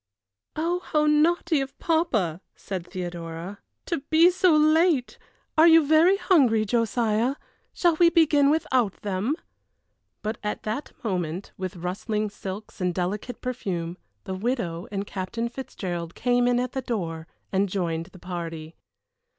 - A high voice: Yes, high, 220 Hz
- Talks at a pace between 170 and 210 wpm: No, average, 140 wpm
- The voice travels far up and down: Yes, wide, 8.5 semitones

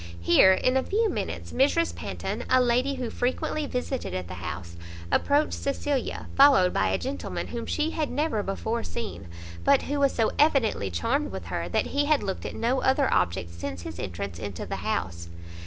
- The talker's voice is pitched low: No, high, 230 Hz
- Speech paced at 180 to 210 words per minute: Yes, average, 190 wpm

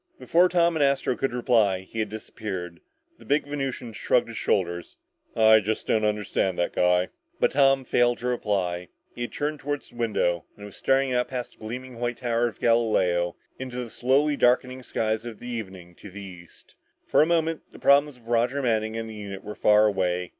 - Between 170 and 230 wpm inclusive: Yes, average, 195 wpm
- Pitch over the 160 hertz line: No, low, 115 Hz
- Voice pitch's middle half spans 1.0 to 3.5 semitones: No, average, 4.2 semitones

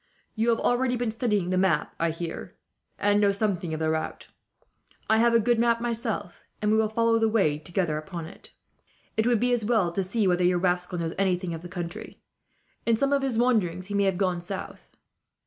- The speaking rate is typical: No, fast, 215 wpm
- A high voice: Yes, high, 200 Hz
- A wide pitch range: No, average, 4.6 semitones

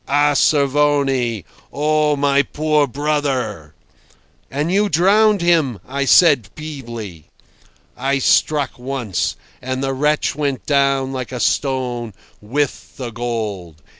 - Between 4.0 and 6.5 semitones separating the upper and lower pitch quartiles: No, average, 3.4 semitones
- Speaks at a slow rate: Yes, slow, 115 wpm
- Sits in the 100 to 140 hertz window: Yes, low, 135 Hz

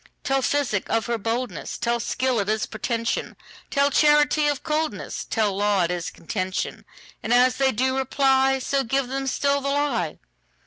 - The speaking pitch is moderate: No, very high, 255 Hz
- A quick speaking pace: No, average, 140 wpm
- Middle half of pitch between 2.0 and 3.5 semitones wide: No, average, 4.1 semitones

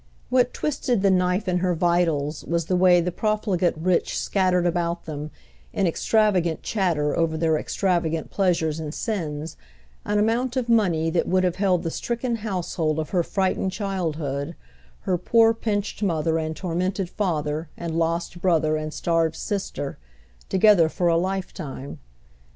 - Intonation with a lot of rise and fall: No, average, 3.3 semitones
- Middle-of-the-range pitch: Yes, medium, 175 Hz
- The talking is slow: No, average, 150 wpm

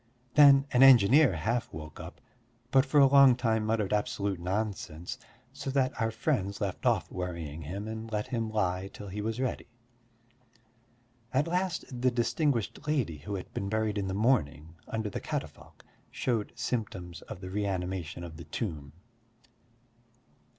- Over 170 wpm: No, average, 155 wpm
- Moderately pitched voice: No, low, 105 Hz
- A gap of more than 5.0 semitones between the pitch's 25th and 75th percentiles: Yes, wide, 5.4 semitones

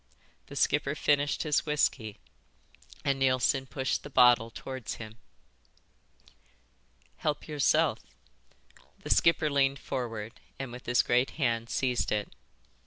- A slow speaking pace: Yes, slow, 115 wpm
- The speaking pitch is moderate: No, low, 130 Hz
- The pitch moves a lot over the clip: No, average, 3.2 semitones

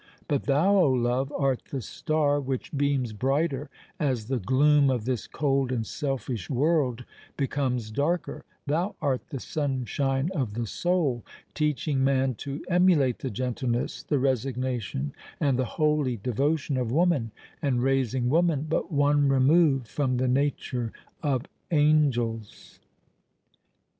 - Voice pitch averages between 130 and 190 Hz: Yes, low, 135 Hz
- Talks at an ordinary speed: No, slow, 125 wpm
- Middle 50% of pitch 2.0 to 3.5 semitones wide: Yes, average, 2.8 semitones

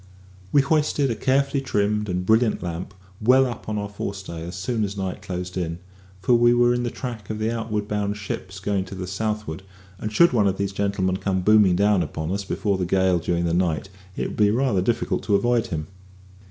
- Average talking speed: No, fast, 220 wpm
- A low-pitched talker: Yes, low, 100 Hz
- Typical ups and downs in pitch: Yes, average, 3.4 semitones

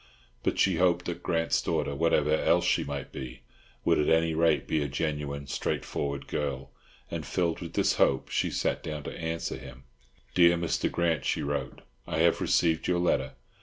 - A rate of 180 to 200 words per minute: Yes, average, 185 wpm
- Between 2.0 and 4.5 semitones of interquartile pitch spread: Yes, average, 2.9 semitones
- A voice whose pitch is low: Yes, very low, 80 Hz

